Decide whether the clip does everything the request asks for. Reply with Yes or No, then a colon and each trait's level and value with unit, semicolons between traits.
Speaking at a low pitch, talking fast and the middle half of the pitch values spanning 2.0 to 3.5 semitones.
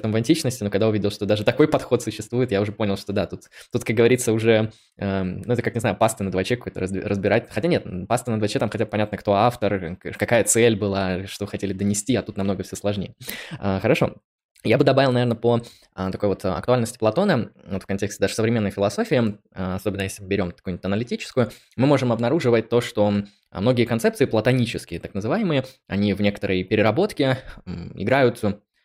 Yes: low, 105 Hz; fast, 190 wpm; average, 3.2 semitones